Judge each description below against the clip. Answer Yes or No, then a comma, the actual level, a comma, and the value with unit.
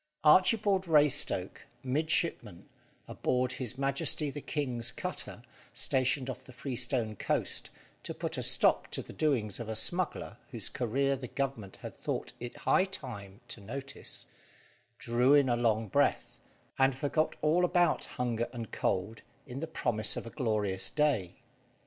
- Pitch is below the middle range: Yes, low, 130 Hz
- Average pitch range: Yes, average, 4.2 semitones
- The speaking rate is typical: Yes, average, 150 wpm